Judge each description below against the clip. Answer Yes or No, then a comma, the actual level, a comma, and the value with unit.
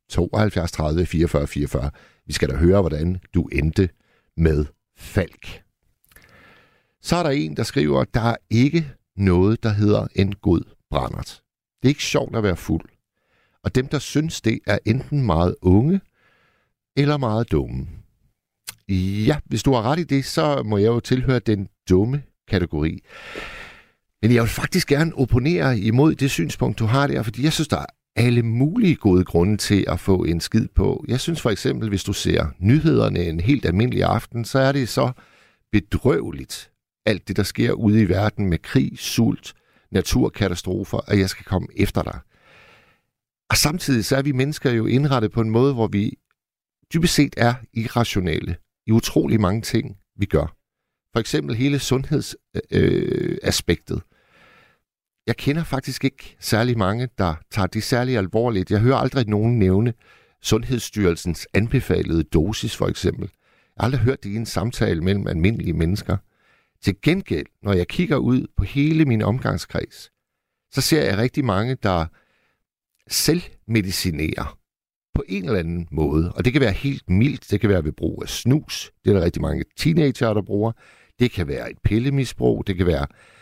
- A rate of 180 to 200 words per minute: No, average, 170 wpm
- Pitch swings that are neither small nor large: No, wide, 5.9 semitones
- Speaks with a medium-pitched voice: No, low, 110 Hz